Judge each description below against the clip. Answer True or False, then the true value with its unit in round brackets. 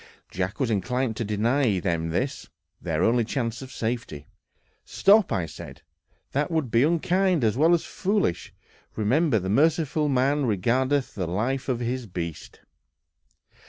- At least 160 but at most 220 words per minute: False (145 wpm)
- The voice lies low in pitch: True (125 Hz)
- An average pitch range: False (5.7 semitones)